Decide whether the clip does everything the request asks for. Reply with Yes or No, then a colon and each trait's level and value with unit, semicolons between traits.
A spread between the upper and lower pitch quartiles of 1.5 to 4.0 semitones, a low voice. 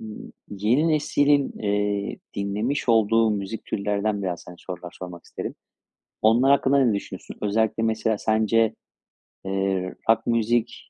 Yes: narrow, 2.4 semitones; low, 110 Hz